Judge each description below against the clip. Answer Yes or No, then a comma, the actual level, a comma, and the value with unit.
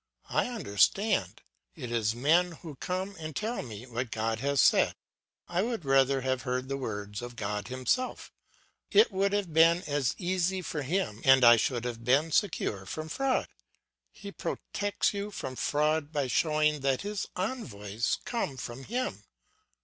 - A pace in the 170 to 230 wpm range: No, average, 160 wpm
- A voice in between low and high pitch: Yes, medium, 145 Hz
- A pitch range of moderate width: No, wide, 7.3 semitones